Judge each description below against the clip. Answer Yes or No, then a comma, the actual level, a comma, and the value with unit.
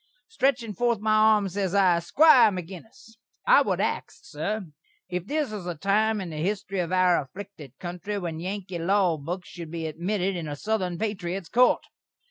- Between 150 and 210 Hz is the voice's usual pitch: Yes, high, 190 Hz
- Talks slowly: No, average, 175 wpm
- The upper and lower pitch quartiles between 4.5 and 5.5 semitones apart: No, average, 3.8 semitones